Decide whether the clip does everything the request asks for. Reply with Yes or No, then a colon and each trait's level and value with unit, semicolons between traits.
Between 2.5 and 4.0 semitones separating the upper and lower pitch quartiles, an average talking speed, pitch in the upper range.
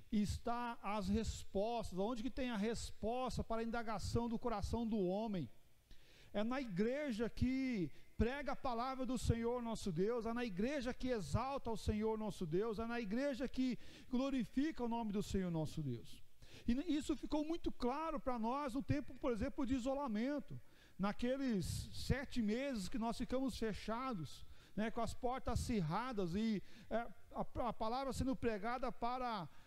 Yes: average, 3.6 semitones; average, 160 wpm; high, 235 Hz